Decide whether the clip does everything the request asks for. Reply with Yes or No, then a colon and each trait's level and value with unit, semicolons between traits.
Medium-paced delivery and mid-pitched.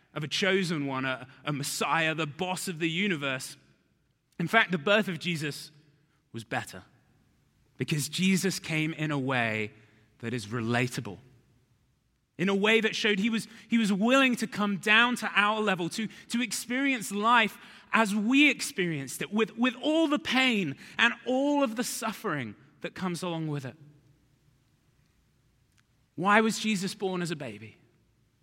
Yes: average, 160 wpm; medium, 180 Hz